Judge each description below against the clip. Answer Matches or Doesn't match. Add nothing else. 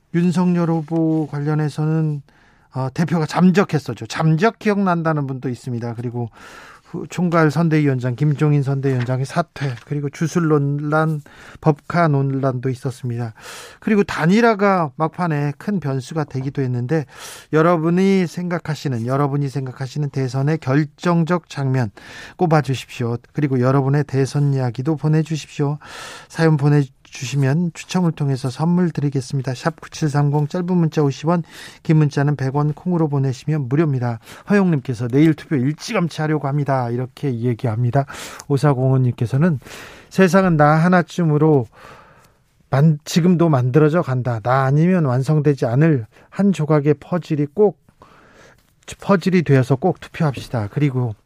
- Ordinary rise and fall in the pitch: Matches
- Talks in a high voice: Doesn't match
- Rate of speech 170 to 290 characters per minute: Doesn't match